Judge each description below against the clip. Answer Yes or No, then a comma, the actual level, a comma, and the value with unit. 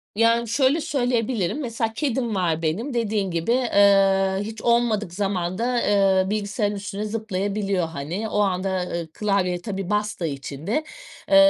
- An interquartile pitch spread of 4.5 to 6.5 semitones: No, average, 3.4 semitones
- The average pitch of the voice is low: No, high, 205 Hz